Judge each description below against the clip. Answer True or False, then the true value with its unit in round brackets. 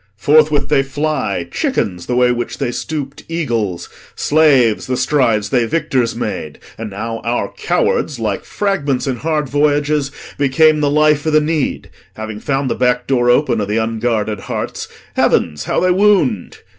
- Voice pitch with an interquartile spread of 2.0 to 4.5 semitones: False (4.9 semitones)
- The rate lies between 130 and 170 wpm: True (160 wpm)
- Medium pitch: False (130 Hz)